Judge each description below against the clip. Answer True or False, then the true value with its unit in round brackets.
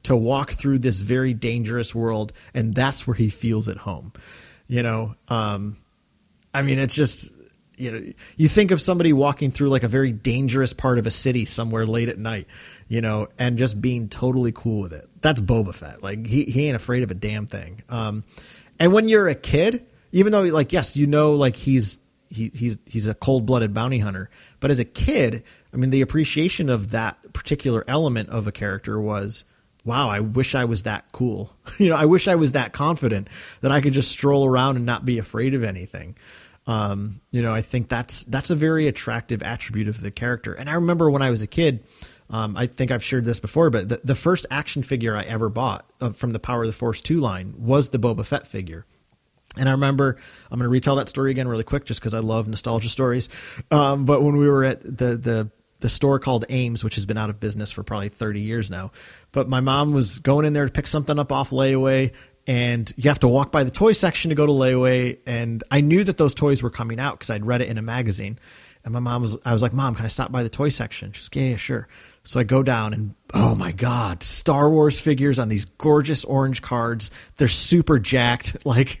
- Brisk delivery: True (230 wpm)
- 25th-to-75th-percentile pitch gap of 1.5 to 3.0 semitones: False (3.7 semitones)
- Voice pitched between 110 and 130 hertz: True (125 Hz)